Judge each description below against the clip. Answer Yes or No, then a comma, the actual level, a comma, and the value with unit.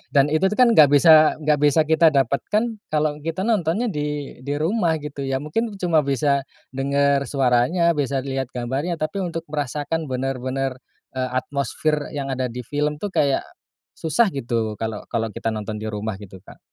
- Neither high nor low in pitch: Yes, medium, 145 Hz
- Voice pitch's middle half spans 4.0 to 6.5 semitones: No, average, 3.5 semitones